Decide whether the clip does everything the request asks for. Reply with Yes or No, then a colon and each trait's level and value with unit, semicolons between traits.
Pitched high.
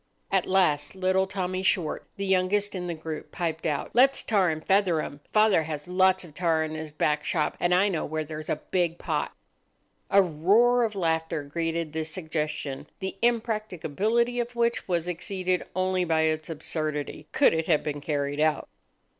No: medium, 175 Hz